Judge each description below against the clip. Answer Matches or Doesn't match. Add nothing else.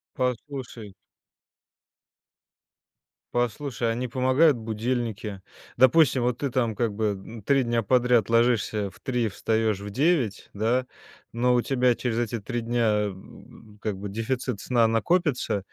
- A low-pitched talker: Matches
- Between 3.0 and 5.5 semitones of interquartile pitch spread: Doesn't match